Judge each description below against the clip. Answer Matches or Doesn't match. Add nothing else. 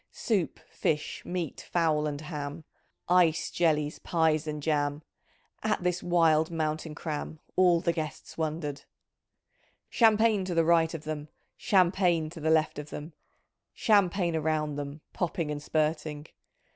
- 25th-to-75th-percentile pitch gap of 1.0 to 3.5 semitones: Matches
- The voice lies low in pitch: Doesn't match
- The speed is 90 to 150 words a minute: Matches